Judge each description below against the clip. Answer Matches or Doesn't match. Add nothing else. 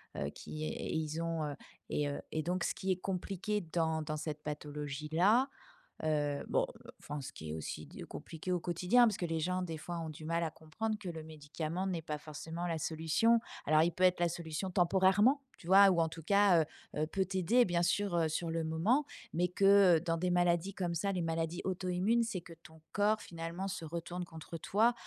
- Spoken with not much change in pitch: Doesn't match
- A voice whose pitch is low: Doesn't match